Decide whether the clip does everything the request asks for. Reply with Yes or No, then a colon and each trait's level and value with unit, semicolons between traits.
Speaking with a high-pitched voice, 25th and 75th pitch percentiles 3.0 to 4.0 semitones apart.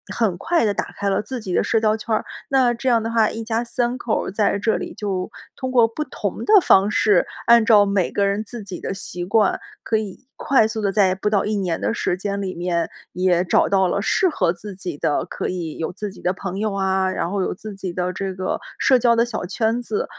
Yes: high, 205 Hz; average, 3.3 semitones